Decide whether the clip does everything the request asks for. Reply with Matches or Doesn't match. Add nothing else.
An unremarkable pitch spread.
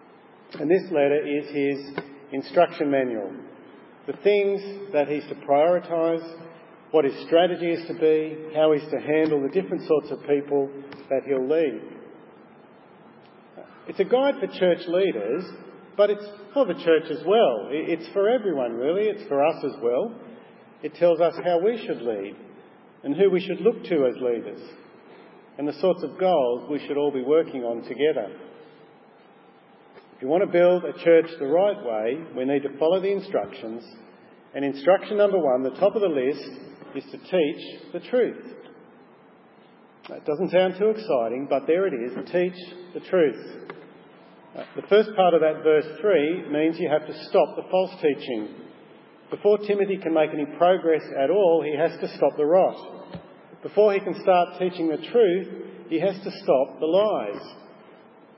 Matches